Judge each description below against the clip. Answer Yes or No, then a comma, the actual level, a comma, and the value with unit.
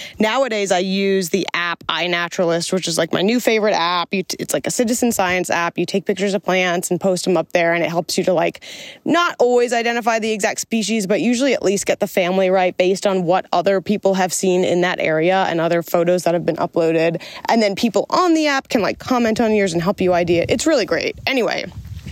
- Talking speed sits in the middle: No, fast, 230 wpm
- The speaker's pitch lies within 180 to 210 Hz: Yes, high, 190 Hz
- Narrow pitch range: No, average, 4.2 semitones